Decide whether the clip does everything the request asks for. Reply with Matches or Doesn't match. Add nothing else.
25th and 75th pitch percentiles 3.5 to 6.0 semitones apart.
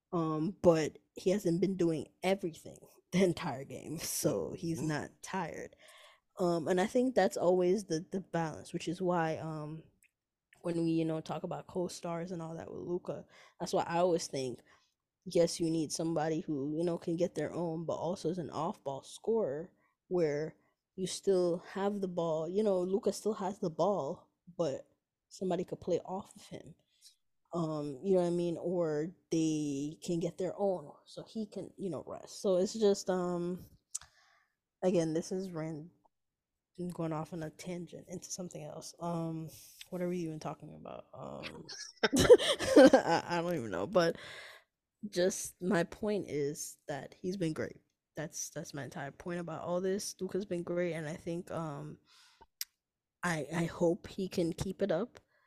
Doesn't match